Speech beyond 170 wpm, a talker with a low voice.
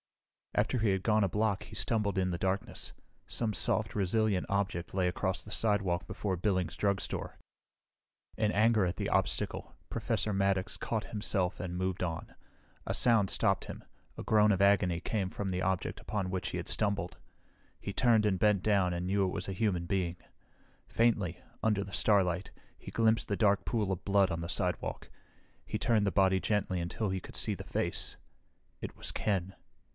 Yes: average, 180 wpm; low, 100 Hz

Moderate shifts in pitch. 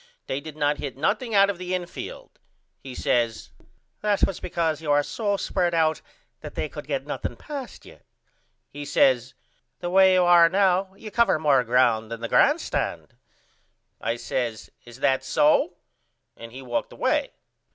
No: wide, 6.4 semitones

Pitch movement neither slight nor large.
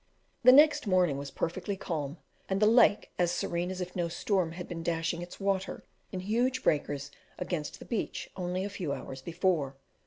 Yes: average, 3.1 semitones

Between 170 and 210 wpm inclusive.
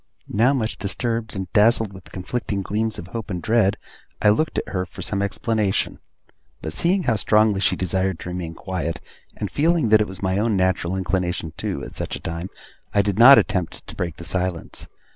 Yes: average, 200 wpm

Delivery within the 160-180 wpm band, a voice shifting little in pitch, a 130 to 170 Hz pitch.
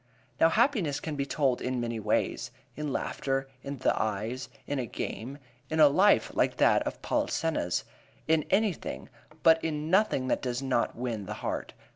No: average, 170 wpm; average, 4.7 semitones; medium, 140 Hz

